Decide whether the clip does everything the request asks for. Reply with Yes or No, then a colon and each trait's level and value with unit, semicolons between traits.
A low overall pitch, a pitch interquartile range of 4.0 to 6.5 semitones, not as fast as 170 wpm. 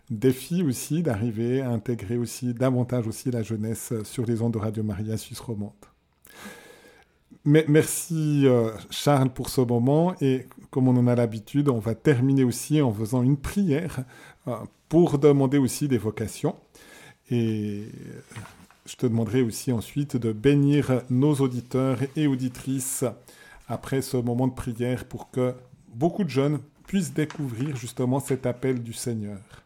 No: low, 130 Hz; average, 3.0 semitones; average, 150 wpm